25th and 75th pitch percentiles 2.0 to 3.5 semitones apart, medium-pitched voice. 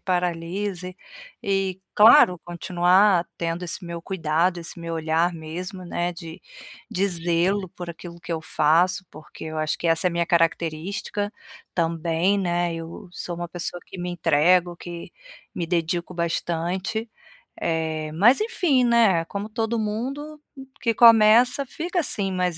Yes: average, 3.1 semitones; medium, 175 Hz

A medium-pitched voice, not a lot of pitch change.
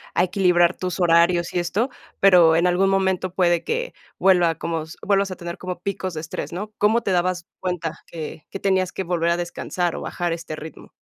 Yes: medium, 180 Hz; narrow, 1.9 semitones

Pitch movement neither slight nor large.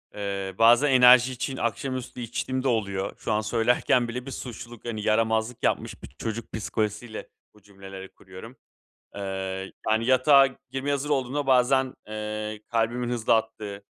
Yes: average, 3.1 semitones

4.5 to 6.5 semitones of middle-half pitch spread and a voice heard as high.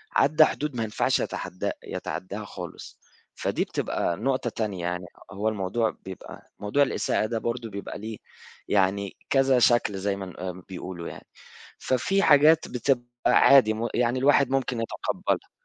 No: average, 5.0 semitones; low, 110 Hz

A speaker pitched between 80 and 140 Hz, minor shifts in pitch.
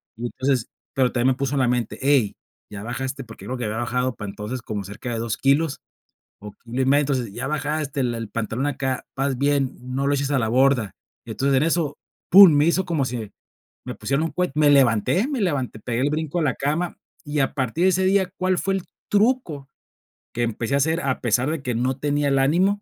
No: low, 135 Hz; average, 3.7 semitones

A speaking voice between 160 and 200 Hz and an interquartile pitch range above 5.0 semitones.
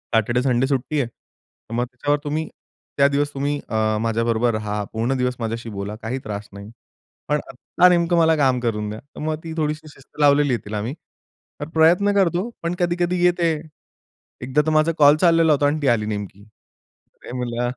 No: low, 135 Hz; wide, 5.5 semitones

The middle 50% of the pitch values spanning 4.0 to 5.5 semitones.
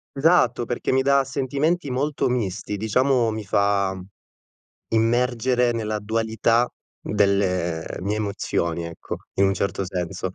Yes: average, 4.3 semitones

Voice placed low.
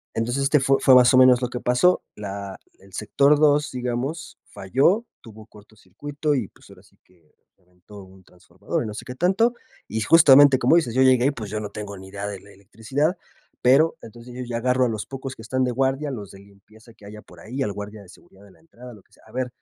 Yes: low, 120 Hz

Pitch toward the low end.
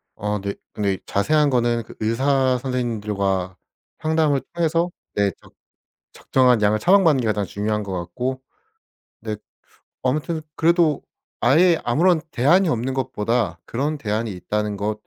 Yes: low, 120 Hz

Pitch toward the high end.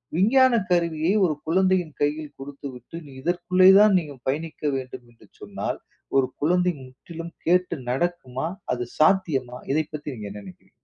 No: medium, 160 Hz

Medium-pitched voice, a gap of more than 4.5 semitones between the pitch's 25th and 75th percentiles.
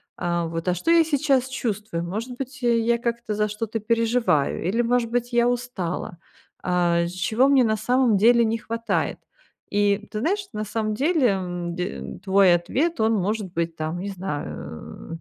No: high, 215 Hz; average, 5.3 semitones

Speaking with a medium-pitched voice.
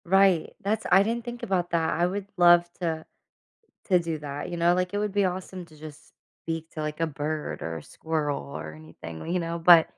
Yes: medium, 170 Hz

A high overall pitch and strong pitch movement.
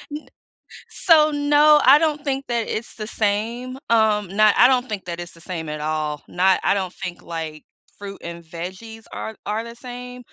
Yes: high, 215 Hz; wide, 6.1 semitones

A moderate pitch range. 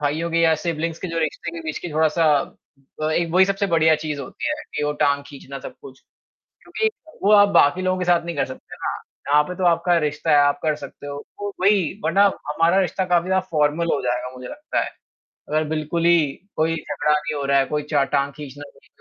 Yes: average, 3.1 semitones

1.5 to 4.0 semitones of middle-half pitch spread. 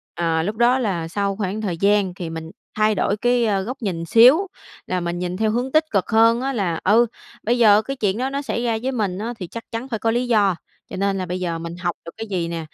No: average, 4.6 semitones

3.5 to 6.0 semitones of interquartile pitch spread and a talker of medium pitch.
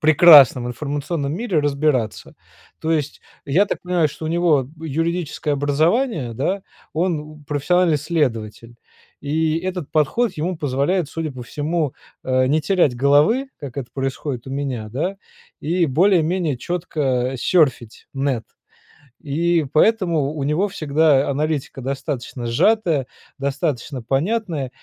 Yes: average, 4.0 semitones; medium, 150 Hz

